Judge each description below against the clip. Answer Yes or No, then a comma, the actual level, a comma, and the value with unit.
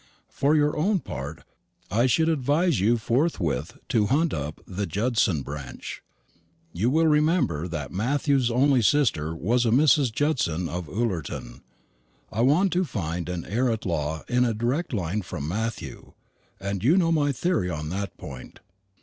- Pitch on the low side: Yes, low, 115 Hz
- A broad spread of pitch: Yes, wide, 8.8 semitones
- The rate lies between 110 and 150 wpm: No, average, 160 wpm